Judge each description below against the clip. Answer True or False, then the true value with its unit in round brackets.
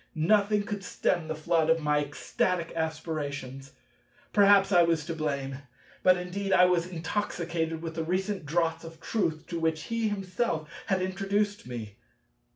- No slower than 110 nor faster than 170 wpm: True (155 wpm)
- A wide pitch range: False (3.5 semitones)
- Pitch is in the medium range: True (165 Hz)